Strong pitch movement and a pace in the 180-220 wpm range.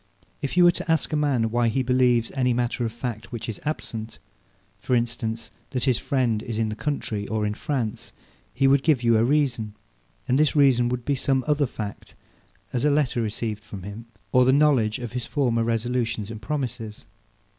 No: average, 3.3 semitones; average, 200 wpm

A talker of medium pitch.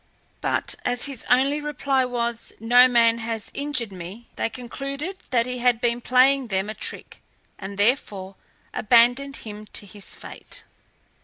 No: high, 240 Hz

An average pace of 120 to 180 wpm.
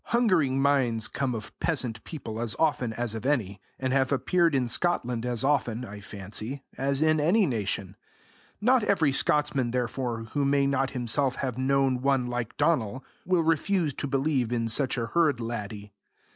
Yes: average, 170 wpm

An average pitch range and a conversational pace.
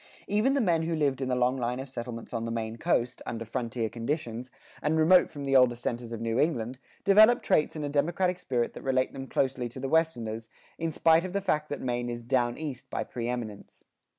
No: average, 4.9 semitones; fast, 220 wpm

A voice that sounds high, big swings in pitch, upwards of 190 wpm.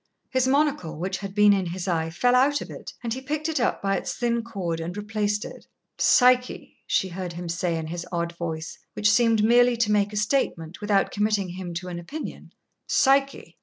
Yes: high, 205 Hz; wide, 5.8 semitones; fast, 205 wpm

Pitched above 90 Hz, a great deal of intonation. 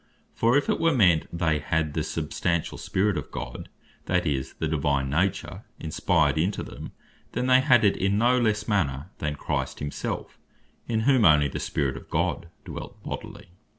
No: very low, 85 Hz; wide, 6.9 semitones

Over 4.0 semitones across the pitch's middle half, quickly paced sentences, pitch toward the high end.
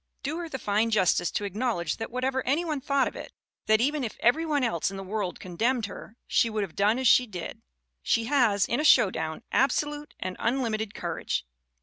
Yes: average, 4.9 semitones; fast, 215 wpm; high, 230 Hz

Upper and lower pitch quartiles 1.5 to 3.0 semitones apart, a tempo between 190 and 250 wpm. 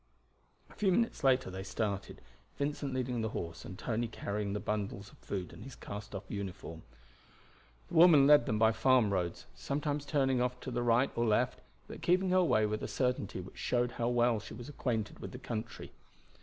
No: average, 4.4 semitones; average, 195 wpm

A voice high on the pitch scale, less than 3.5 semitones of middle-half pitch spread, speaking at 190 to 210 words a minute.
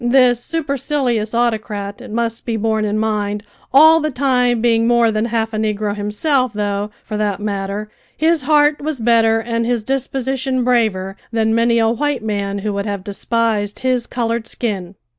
No: high, 230 Hz; average, 3.0 semitones; average, 170 wpm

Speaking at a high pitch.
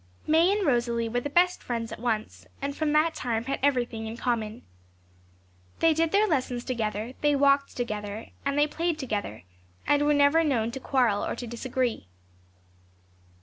Yes: very high, 255 Hz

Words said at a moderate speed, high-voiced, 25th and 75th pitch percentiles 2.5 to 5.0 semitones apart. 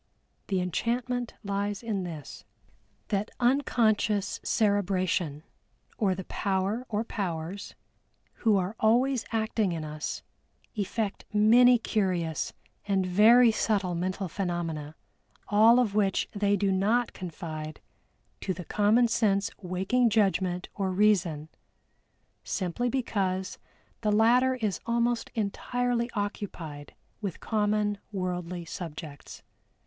No: slow, 110 wpm; high, 200 Hz; average, 3.6 semitones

